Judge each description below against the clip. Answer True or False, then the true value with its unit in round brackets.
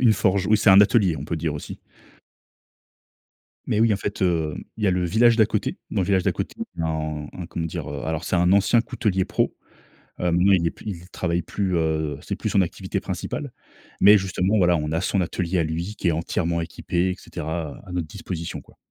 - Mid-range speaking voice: False (90 Hz)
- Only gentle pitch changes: False (3.1 semitones)